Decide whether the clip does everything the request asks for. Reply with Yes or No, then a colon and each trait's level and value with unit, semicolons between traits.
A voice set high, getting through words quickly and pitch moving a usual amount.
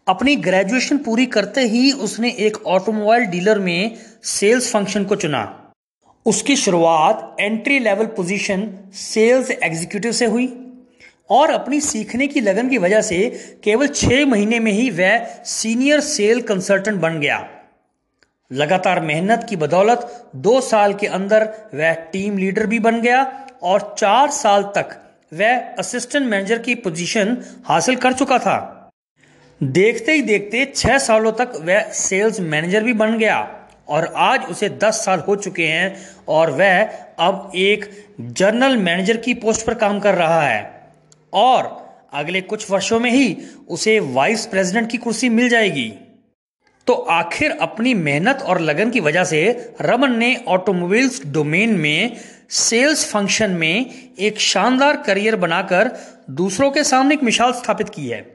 No: high, 220 Hz; average, 150 wpm; average, 3.9 semitones